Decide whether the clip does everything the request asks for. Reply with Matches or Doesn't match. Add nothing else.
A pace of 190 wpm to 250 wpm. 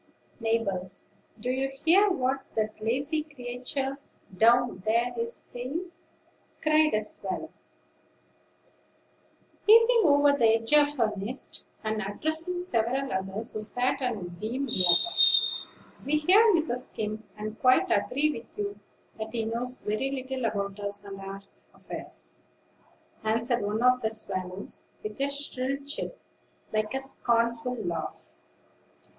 Doesn't match